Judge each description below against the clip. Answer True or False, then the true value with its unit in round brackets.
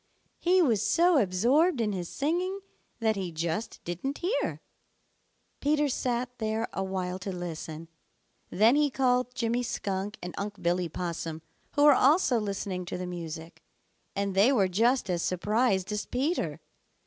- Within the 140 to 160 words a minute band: True (150 wpm)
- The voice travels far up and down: True (6.2 semitones)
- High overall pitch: True (210 Hz)